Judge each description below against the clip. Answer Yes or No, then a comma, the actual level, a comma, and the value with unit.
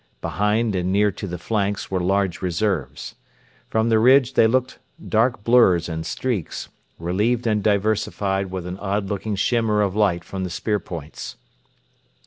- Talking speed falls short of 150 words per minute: No, average, 155 wpm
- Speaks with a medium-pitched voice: No, low, 100 Hz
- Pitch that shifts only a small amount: No, average, 3.1 semitones